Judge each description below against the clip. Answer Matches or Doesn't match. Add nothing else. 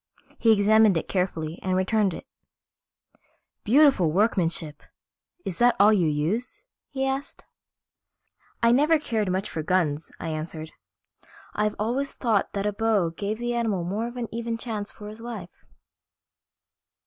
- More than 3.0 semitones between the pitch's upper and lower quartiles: Matches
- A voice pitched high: Matches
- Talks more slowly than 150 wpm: Matches